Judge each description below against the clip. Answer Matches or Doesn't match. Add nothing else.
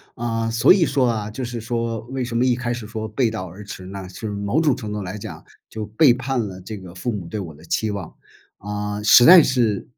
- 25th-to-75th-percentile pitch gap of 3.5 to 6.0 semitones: Doesn't match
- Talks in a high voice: Doesn't match